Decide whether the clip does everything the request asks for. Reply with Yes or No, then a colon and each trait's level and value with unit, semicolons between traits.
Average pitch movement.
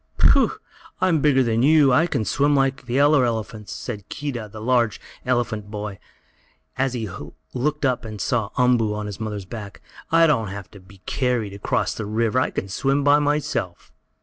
Yes: average, 4.6 semitones